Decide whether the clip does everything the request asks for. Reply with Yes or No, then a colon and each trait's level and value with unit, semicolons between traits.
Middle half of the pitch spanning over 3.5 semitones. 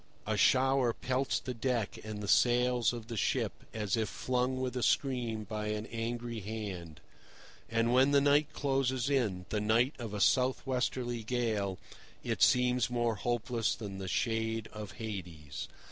No: average, 2.9 semitones